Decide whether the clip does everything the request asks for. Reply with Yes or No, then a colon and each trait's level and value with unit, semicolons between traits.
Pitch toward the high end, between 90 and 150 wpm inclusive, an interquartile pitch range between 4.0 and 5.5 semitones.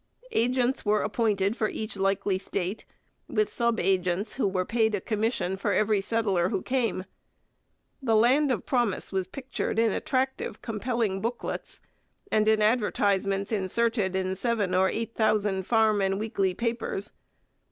No: high, 215 Hz; average, 145 wpm; average, 3.2 semitones